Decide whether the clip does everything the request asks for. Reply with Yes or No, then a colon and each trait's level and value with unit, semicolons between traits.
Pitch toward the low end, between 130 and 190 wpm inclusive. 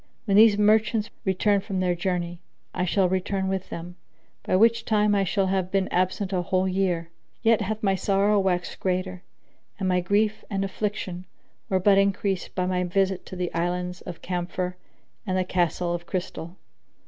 No: high, 190 Hz; average, 175 wpm